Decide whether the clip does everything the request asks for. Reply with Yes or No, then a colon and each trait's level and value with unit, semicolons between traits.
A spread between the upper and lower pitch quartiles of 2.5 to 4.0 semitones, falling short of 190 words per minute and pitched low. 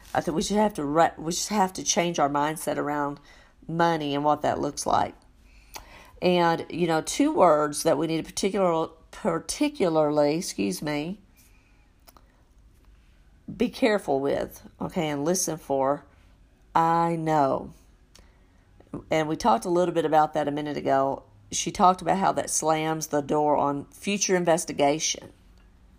No: average, 3.1 semitones; average, 150 wpm; medium, 155 Hz